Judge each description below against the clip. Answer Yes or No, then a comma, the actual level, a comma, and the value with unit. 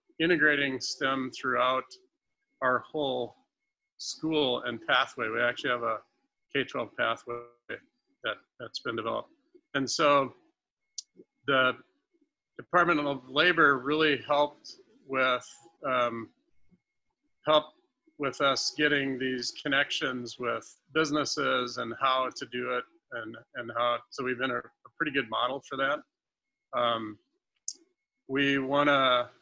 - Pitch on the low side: No, medium, 145 Hz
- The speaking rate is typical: No, slow, 120 wpm